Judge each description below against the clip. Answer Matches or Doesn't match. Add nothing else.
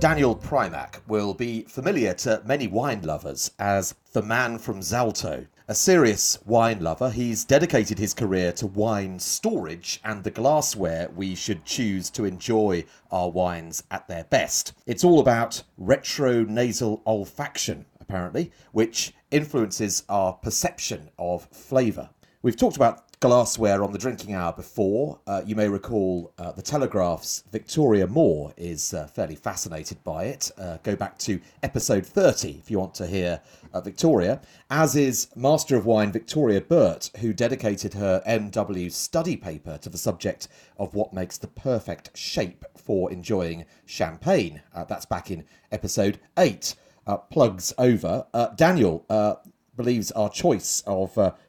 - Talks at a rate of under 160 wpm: Matches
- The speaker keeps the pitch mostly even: Doesn't match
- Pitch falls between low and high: Doesn't match